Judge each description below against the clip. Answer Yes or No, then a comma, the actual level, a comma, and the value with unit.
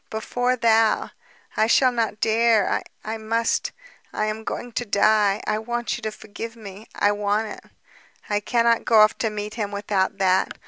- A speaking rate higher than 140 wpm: Yes, average, 175 wpm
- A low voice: No, high, 220 Hz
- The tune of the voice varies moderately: No, narrow, 1.7 semitones